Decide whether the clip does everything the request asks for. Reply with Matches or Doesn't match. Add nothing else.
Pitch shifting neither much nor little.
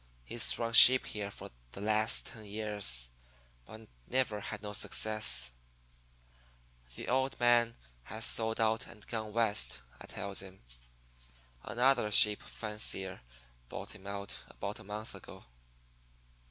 Doesn't match